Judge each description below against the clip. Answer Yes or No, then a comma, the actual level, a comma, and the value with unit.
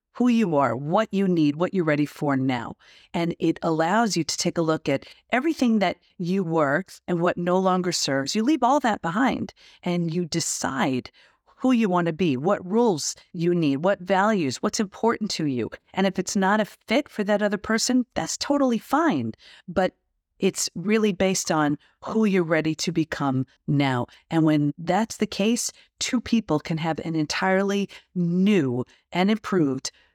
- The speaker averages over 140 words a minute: Yes, average, 180 wpm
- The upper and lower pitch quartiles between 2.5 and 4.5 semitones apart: No, average, 5.1 semitones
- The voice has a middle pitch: Yes, medium, 180 Hz